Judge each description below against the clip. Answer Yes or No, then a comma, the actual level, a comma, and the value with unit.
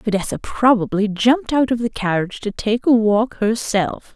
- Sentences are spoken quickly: No, average, 175 wpm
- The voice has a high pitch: Yes, high, 220 Hz